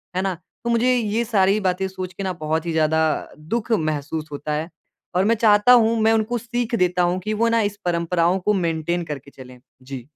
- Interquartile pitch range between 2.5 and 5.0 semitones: No, wide, 5.5 semitones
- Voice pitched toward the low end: No, medium, 185 Hz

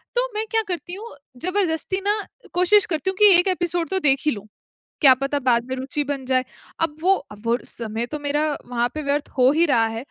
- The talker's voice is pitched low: No, very high, 300 Hz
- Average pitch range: No, wide, 6.2 semitones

